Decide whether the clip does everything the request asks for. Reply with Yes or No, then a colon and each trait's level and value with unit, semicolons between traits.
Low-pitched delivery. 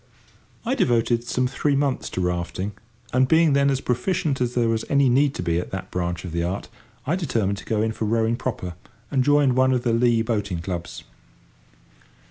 Yes: low, 120 Hz